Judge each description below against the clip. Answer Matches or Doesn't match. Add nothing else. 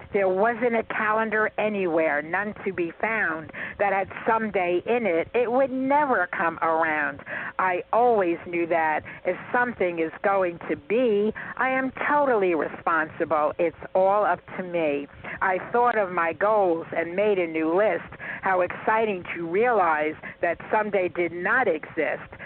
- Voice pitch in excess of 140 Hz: Matches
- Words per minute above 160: Doesn't match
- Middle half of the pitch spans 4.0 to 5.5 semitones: Matches